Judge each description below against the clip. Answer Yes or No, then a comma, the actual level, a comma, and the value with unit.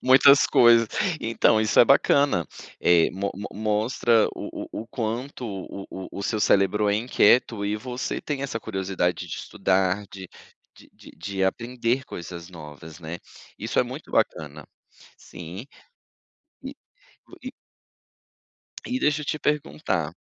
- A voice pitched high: No, low, 105 Hz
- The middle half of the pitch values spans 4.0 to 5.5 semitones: Yes, average, 4.8 semitones